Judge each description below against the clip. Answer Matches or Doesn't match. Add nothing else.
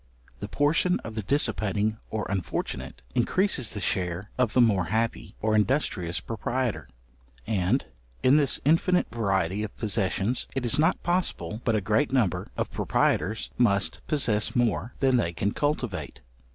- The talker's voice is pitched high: Doesn't match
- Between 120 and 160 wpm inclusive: Matches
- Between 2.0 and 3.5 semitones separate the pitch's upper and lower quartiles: Doesn't match